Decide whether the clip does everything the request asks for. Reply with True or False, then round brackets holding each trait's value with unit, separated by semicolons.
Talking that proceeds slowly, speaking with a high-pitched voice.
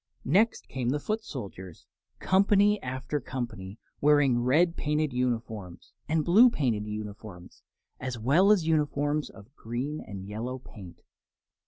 False (130 wpm; 130 Hz)